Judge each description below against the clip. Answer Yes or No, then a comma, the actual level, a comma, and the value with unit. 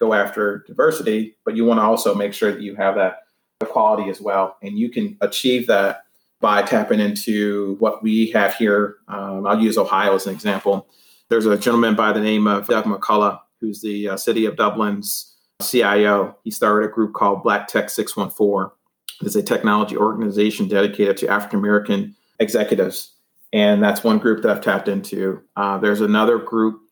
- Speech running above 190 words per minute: No, average, 180 wpm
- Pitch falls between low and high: No, low, 105 Hz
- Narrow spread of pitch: Yes, narrow, 2.1 semitones